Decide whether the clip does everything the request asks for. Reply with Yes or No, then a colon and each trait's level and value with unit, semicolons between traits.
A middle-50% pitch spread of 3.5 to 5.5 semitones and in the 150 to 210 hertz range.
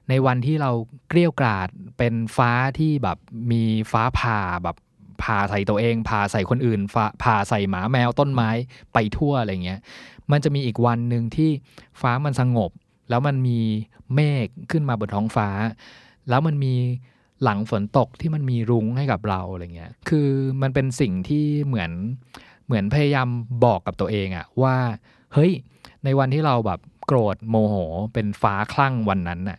No: average, 4.1 semitones; low, 120 Hz